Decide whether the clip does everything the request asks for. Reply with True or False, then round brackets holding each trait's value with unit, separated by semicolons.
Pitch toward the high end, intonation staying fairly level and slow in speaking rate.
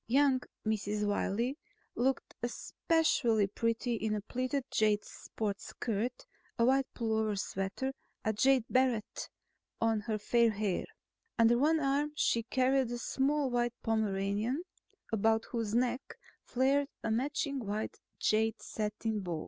False (230 Hz; 3.5 semitones; 130 wpm)